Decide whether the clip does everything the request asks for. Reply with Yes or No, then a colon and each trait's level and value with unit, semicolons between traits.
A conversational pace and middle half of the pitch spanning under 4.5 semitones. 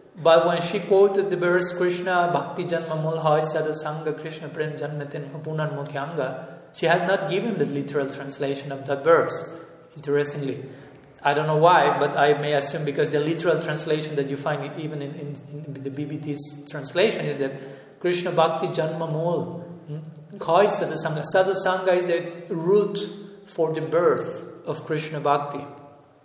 Yes: average, 155 wpm; average, 3.0 semitones